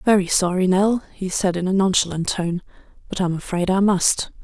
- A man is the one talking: No, female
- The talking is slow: No, average, 190 wpm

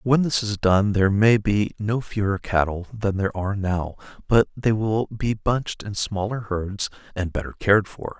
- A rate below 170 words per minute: No, average, 190 wpm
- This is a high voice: No, low, 105 Hz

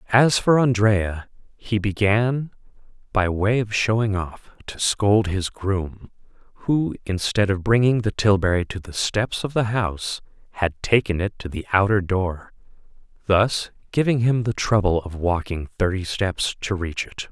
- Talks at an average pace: Yes, average, 155 wpm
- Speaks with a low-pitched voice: Yes, low, 100 Hz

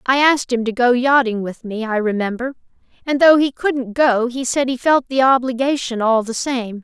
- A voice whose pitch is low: No, very high, 250 Hz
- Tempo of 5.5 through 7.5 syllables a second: No, 5.0 syllables/s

